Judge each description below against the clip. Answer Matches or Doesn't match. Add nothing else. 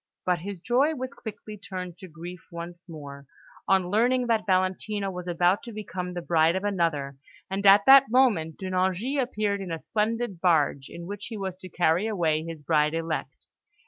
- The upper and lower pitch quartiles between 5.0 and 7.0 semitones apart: Doesn't match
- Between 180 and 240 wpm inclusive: Matches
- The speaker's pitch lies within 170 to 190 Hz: Matches